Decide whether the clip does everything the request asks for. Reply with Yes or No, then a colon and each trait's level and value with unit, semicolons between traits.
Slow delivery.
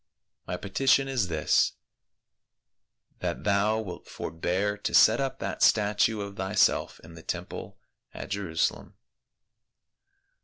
Yes: slow, 115 wpm